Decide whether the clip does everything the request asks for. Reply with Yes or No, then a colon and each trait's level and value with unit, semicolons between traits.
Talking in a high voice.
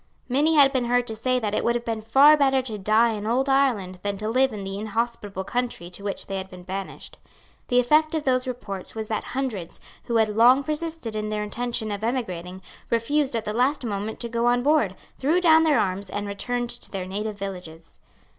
Yes: high, 230 Hz